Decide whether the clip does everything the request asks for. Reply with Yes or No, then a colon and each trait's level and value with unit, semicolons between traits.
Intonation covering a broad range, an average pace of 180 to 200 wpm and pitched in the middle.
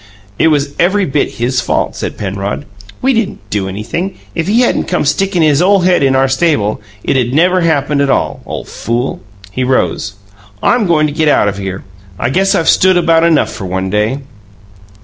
Yes: wide, 7.1 semitones; average, 190 wpm; medium, 145 Hz